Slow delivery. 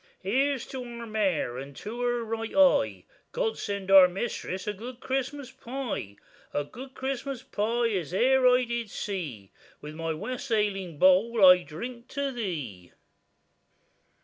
No: average, 145 wpm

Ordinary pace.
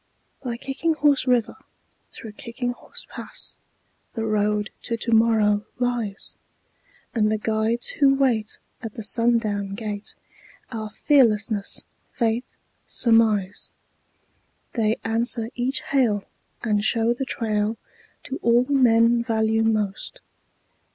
No: slow, 110 wpm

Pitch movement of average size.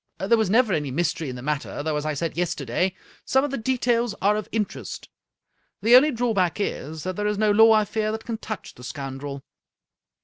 No: wide, 6.6 semitones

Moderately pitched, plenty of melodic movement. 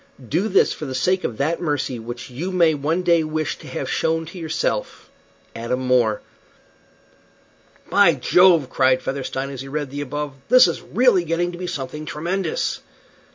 No: medium, 155 Hz; average, 4.8 semitones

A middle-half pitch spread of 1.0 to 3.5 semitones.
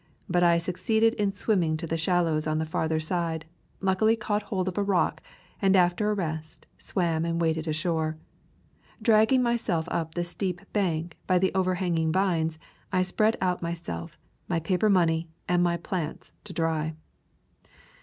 Yes: average, 2.9 semitones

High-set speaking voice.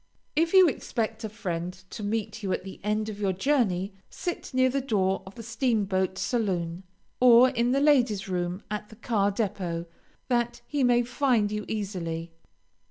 Yes: high, 215 Hz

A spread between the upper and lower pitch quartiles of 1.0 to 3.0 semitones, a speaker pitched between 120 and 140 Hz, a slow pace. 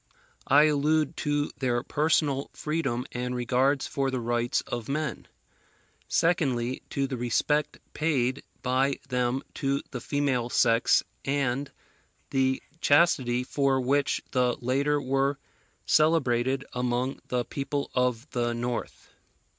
Yes: narrow, 2.5 semitones; low, 135 Hz; slow, 120 wpm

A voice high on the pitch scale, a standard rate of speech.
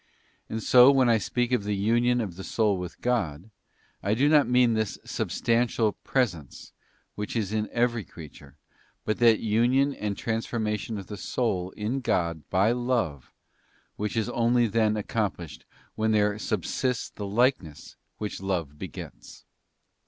No: low, 110 Hz; average, 155 wpm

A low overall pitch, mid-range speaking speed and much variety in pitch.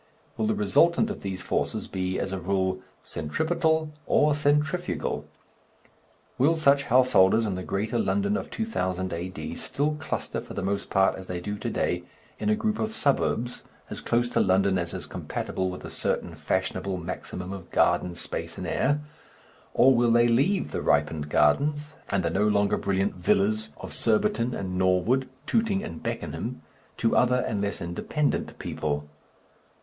Yes: low, 110 Hz; average, 165 wpm; wide, 8.0 semitones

